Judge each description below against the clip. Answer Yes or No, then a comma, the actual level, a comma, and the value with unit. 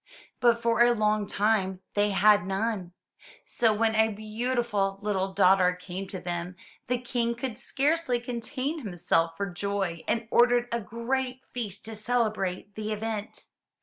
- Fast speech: No, average, 150 wpm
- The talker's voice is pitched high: Yes, high, 215 Hz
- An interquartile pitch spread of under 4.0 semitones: Yes, average, 3.4 semitones